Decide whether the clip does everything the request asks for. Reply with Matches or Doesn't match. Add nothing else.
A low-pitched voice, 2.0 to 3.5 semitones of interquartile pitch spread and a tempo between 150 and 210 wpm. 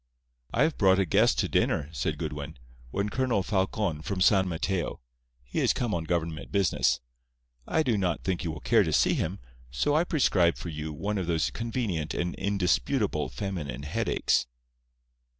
Doesn't match